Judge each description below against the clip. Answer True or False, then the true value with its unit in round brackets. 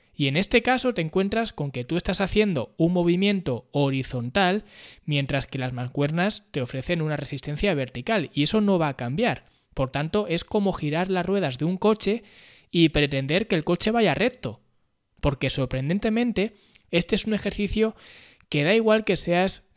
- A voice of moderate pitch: True (175 Hz)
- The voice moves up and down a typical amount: False (6.2 semitones)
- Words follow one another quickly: False (175 wpm)